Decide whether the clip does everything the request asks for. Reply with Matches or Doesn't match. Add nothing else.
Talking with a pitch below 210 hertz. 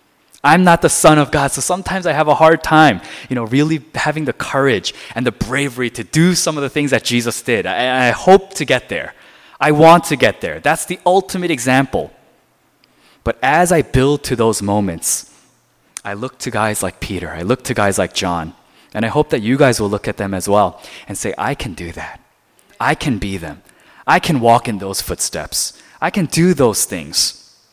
Matches